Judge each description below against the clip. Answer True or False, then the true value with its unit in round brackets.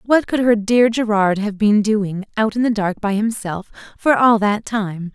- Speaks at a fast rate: True (210 wpm)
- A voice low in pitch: False (215 Hz)